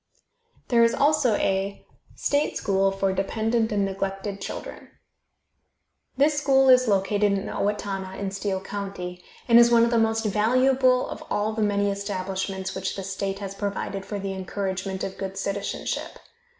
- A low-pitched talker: No, high, 200 Hz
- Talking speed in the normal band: Yes, average, 155 wpm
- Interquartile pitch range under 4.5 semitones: Yes, narrow, 2.6 semitones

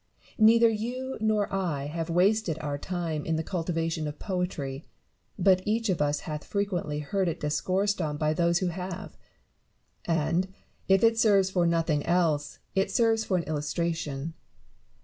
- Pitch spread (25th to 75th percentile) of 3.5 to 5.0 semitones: Yes, average, 4.1 semitones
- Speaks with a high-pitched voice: No, medium, 175 Hz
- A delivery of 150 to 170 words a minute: Yes, average, 160 wpm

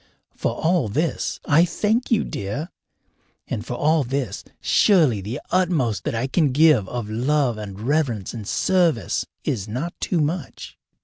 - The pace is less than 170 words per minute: Yes, average, 150 wpm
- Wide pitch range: Yes, wide, 6.6 semitones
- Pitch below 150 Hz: Yes, medium, 140 Hz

